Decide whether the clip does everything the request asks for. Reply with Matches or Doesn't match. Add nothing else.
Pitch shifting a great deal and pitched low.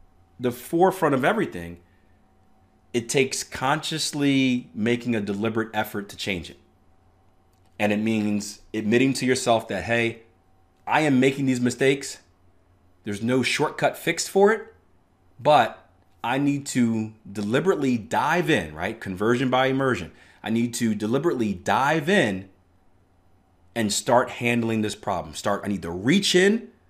Matches